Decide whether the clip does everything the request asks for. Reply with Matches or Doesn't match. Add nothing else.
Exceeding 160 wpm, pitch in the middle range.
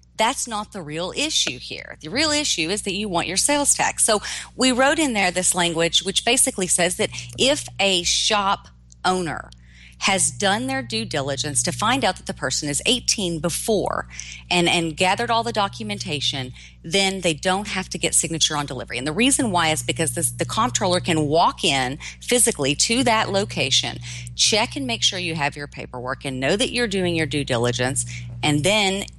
Matches